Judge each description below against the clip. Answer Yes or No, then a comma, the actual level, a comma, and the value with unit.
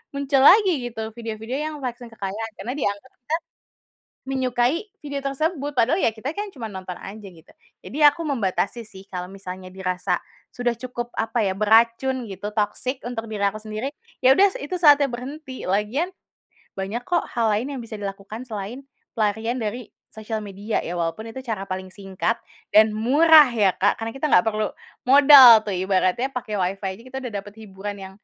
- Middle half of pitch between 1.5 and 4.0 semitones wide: No, average, 4.6 semitones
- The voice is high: Yes, high, 225 Hz